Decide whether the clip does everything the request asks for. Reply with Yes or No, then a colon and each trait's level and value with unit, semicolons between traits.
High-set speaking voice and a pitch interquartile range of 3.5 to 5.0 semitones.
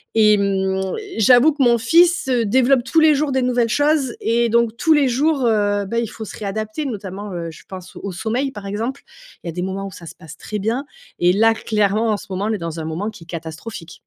Yes: high, 220 Hz; average, 4.6 semitones